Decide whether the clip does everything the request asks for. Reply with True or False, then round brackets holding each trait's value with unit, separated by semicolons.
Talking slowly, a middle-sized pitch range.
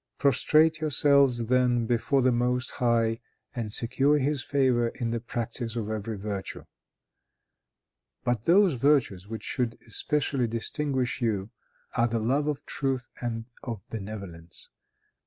True (130 wpm; 3.4 semitones)